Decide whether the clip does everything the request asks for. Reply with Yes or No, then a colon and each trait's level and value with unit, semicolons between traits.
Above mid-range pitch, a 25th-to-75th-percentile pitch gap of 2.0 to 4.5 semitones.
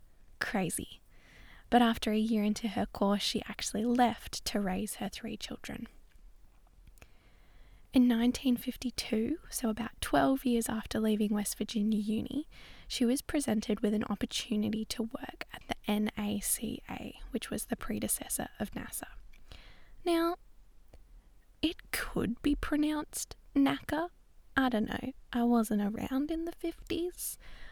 Yes: high, 235 Hz; average, 3.9 semitones